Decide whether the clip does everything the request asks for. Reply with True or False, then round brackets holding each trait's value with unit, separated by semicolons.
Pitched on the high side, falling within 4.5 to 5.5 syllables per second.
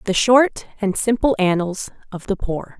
False (205 Hz; 4.3 syllables/s)